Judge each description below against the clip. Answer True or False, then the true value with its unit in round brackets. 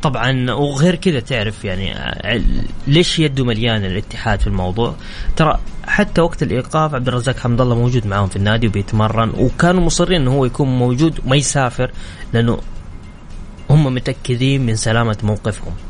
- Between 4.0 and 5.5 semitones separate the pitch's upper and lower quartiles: True (4.6 semitones)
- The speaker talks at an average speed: False (145 wpm)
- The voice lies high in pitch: False (120 Hz)